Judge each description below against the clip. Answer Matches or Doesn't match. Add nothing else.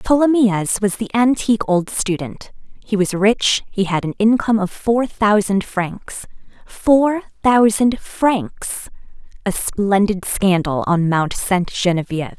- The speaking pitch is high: Matches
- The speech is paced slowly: Matches